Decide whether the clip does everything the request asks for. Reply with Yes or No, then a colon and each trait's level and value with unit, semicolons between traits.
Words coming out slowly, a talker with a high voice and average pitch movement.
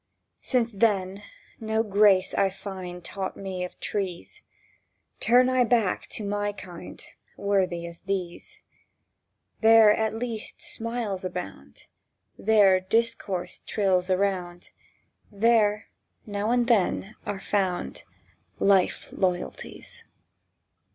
Yes: slow, 105 wpm; high, 200 Hz; average, 3.1 semitones